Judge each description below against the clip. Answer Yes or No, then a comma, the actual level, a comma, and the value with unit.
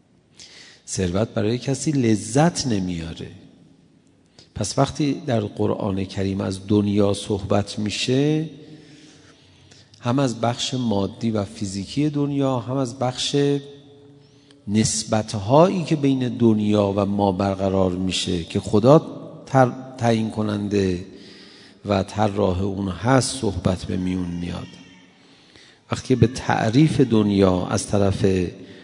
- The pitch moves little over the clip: No, wide, 5.4 semitones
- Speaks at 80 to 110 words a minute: Yes, slow, 105 wpm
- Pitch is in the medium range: No, low, 110 Hz